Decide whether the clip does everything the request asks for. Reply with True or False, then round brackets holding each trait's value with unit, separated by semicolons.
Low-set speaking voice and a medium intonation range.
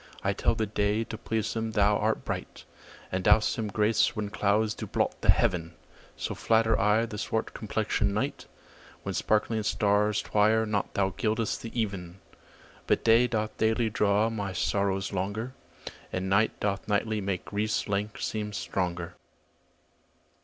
False (105 Hz; 1.8 semitones)